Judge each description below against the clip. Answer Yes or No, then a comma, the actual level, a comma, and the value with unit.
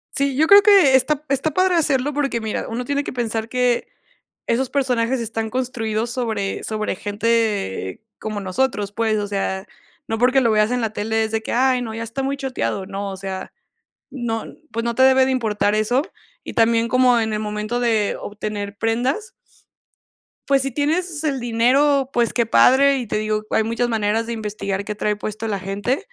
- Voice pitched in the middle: No, high, 230 Hz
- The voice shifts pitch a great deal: No, average, 3.7 semitones